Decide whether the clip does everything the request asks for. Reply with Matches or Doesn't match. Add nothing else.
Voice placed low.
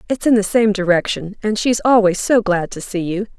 Doesn't match